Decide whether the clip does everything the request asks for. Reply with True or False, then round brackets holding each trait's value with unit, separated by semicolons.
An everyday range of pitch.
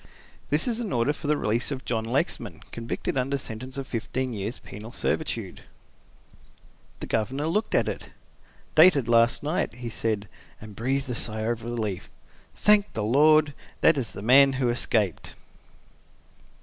True (4.1 semitones)